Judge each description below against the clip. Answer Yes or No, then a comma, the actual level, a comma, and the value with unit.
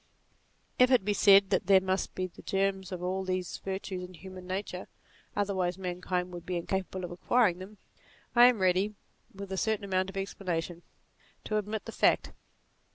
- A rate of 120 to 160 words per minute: No, average, 175 wpm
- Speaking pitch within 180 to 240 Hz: Yes, high, 190 Hz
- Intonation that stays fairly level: Yes, narrow, 1.6 semitones